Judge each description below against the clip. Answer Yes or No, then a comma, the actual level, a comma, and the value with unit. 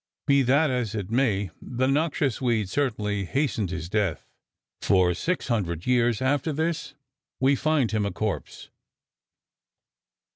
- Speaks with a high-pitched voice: No, low, 120 Hz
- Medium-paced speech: No, slow, 125 wpm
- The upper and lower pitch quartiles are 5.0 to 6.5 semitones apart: Yes, wide, 5.4 semitones